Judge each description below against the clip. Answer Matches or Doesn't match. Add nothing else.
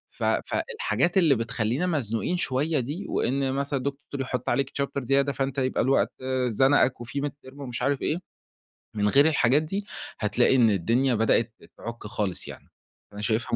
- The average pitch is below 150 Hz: Matches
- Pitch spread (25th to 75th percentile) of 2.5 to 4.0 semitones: Matches